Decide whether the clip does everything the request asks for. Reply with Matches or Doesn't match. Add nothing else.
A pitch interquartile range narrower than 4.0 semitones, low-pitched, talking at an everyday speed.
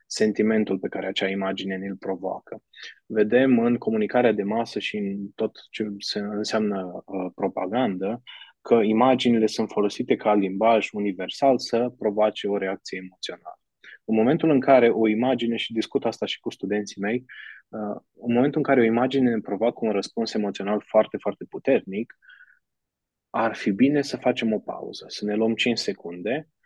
Matches